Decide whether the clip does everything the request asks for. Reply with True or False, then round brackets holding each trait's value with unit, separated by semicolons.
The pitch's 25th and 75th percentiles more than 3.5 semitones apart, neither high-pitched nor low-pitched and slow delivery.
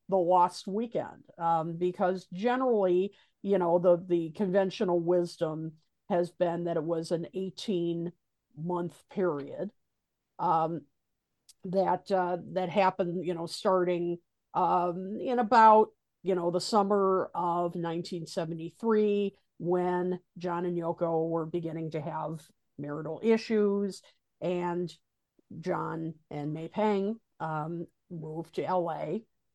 False (2.4 semitones; 175 Hz; 120 wpm)